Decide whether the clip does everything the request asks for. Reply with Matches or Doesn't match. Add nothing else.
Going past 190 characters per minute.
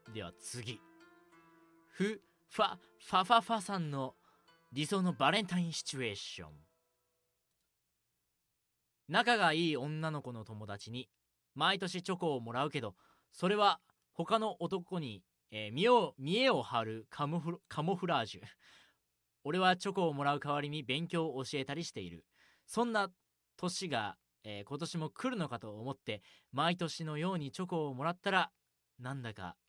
Matches